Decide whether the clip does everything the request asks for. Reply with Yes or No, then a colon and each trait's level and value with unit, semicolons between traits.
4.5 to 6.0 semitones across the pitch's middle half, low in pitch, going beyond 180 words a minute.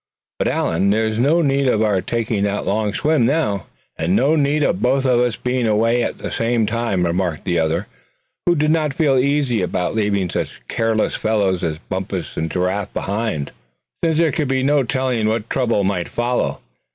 Yes: average, 5.2 semitones; low, 115 Hz; average, 190 wpm